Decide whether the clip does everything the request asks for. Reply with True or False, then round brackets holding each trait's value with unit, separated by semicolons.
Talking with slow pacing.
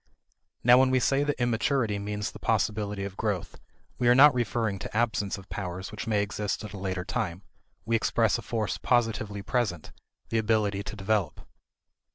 False (180 wpm)